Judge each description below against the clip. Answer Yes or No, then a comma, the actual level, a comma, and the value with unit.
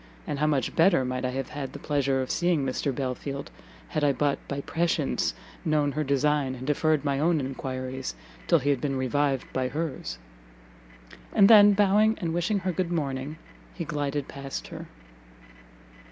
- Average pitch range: Yes, average, 3.3 semitones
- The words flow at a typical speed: Yes, average, 170 wpm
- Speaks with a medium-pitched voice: Yes, medium, 145 Hz